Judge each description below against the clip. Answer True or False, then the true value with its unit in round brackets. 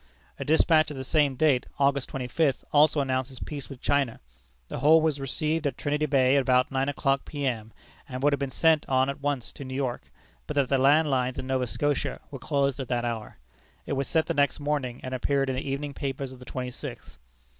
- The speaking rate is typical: False (220 wpm)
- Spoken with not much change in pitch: True (2.0 semitones)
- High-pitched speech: False (135 Hz)